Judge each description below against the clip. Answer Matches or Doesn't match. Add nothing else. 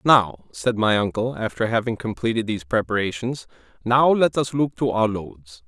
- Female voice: Doesn't match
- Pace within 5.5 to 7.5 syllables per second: Doesn't match